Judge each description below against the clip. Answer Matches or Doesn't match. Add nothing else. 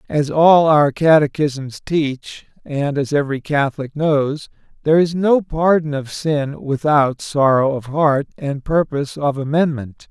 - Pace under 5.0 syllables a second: Matches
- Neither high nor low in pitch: Matches